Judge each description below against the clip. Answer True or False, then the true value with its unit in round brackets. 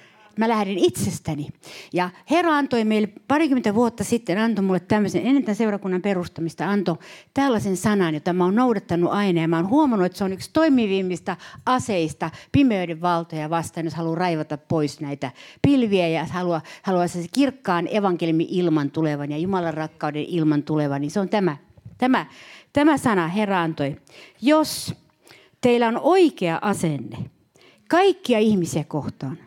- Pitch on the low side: False (180 Hz)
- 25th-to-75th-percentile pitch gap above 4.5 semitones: True (5.4 semitones)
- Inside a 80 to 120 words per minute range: False (150 wpm)